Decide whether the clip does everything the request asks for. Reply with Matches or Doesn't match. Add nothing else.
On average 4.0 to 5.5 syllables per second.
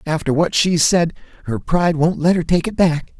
Matches